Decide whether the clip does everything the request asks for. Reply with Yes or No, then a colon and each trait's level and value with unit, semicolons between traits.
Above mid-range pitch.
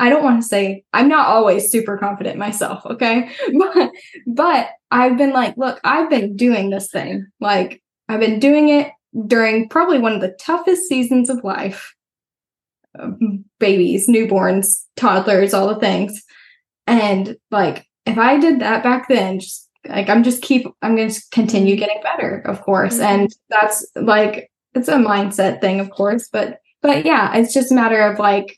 Yes: high, 225 Hz